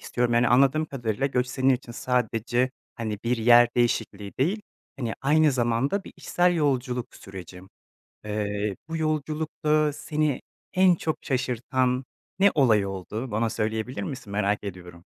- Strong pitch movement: No, average, 4.7 semitones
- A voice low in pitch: Yes, low, 125 Hz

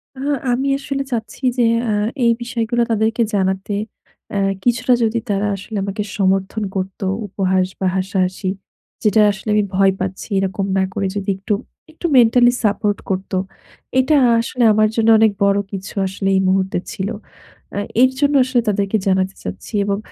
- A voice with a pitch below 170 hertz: No, high, 205 Hz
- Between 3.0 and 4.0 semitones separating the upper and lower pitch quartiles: Yes, average, 3.3 semitones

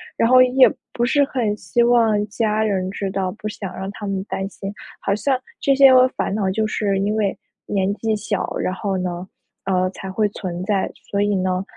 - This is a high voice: Yes, high, 205 Hz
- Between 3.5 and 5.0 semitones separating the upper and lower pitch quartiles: No, average, 2.7 semitones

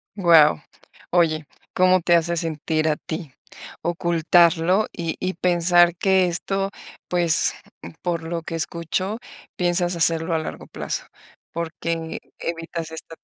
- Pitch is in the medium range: Yes, medium, 170 Hz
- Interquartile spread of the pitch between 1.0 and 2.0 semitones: Yes, narrow, 1.5 semitones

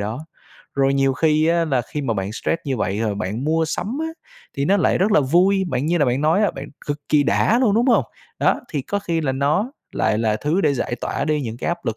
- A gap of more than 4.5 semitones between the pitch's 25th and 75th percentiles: Yes, average, 5.0 semitones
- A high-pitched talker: No, medium, 150 Hz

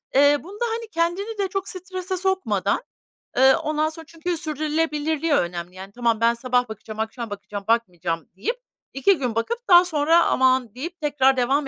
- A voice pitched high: Yes, very high, 295 Hz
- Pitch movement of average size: No, wide, 7.0 semitones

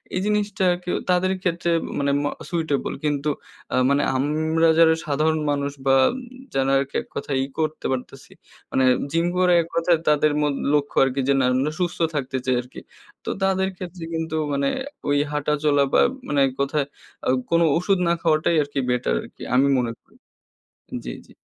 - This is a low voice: No, medium, 150 Hz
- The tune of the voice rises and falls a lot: No, average, 3.3 semitones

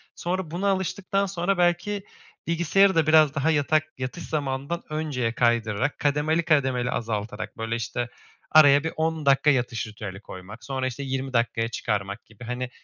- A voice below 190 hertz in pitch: Yes, medium, 140 Hz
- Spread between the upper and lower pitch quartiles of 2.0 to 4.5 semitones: No, wide, 5.5 semitones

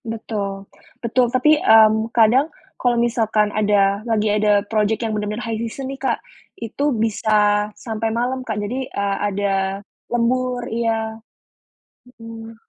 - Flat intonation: Yes, narrow, 2.1 semitones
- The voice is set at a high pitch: Yes, high, 225 Hz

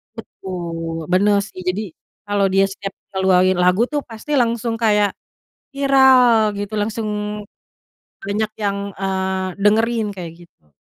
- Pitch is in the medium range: No, high, 205 Hz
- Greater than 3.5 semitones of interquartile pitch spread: No, average, 3.0 semitones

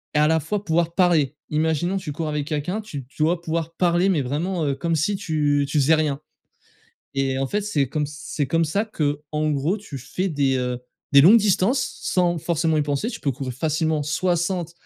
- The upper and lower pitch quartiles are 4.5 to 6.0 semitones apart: No, average, 3.3 semitones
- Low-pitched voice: No, medium, 155 Hz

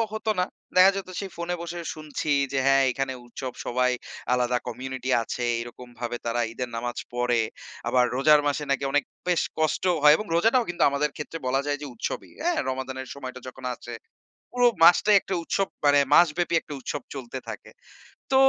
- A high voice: No, medium, 140 Hz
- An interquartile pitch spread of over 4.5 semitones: Yes, average, 5.1 semitones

